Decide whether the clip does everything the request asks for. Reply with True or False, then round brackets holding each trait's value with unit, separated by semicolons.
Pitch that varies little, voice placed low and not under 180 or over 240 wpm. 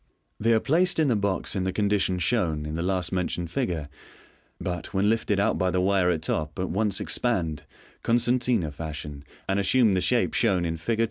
False (4.8 semitones; 95 Hz; 195 wpm)